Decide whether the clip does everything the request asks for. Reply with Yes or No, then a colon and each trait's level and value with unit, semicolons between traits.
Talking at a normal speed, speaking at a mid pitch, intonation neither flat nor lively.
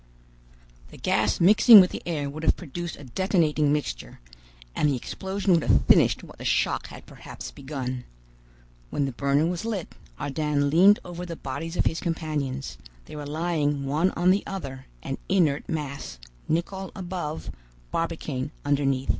Yes: average, 160 wpm; medium, 155 Hz; average, 3.9 semitones